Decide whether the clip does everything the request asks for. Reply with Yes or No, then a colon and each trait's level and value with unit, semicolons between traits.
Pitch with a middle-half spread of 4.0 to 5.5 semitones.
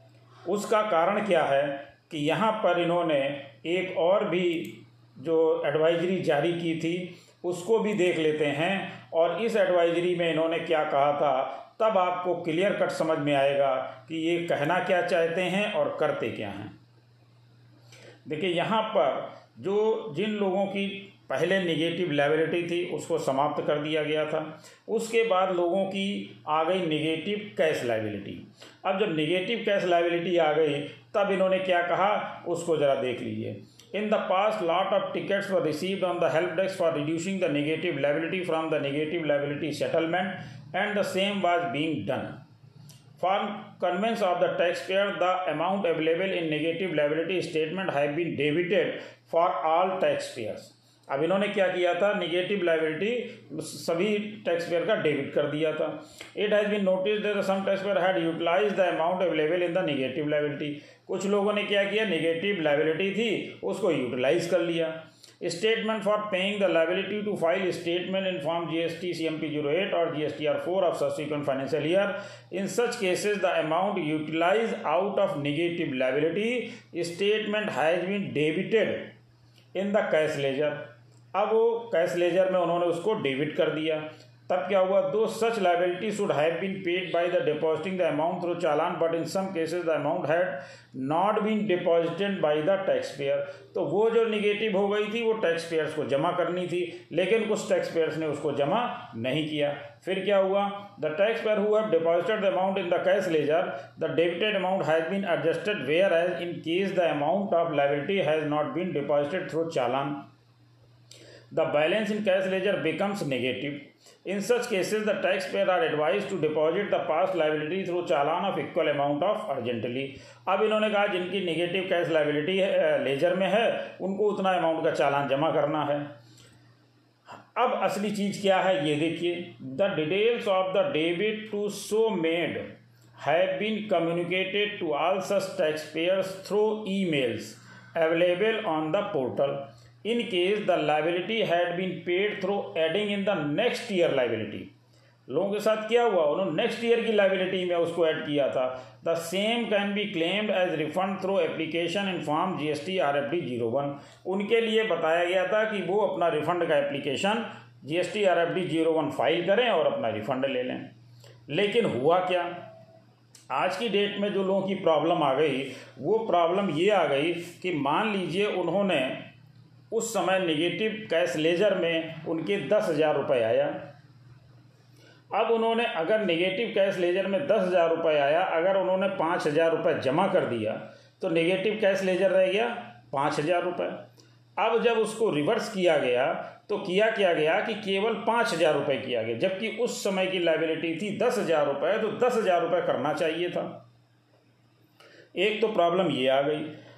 Yes: average, 4.3 semitones